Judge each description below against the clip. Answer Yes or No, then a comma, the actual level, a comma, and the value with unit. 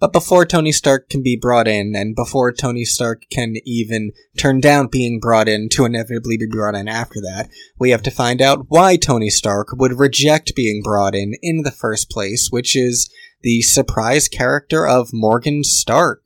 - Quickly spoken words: No, average, 190 wpm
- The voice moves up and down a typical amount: Yes, average, 3.8 semitones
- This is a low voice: Yes, low, 120 Hz